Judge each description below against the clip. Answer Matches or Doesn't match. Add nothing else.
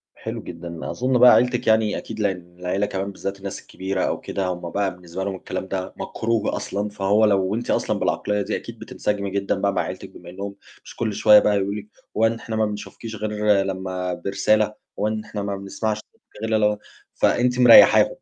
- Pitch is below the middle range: Matches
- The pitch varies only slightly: Matches